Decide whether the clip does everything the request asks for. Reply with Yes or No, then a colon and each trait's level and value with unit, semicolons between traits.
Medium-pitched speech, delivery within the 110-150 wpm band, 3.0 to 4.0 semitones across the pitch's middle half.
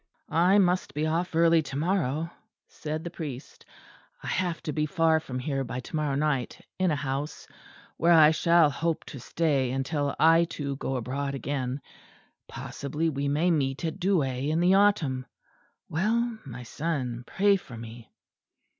No: medium, 150 Hz; average, 165 wpm; average, 3.7 semitones